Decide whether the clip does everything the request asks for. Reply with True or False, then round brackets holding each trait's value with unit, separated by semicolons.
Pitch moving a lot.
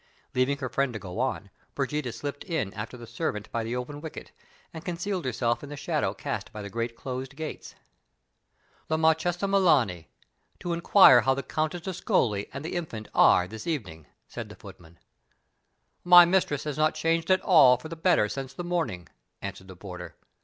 True (6.6 semitones)